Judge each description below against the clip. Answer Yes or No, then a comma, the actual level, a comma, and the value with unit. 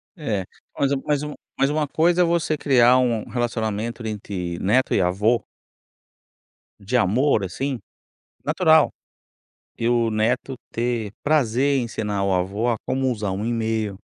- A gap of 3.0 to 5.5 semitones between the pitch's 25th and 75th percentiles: Yes, average, 4.3 semitones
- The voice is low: Yes, low, 115 Hz